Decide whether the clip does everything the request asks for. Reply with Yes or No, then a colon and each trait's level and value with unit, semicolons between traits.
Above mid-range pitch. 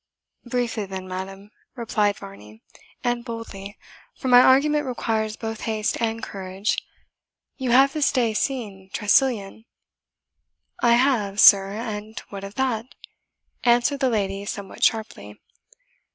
Yes: high, 220 Hz